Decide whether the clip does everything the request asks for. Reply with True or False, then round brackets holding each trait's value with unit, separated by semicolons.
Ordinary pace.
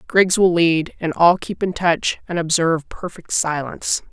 True (175 wpm)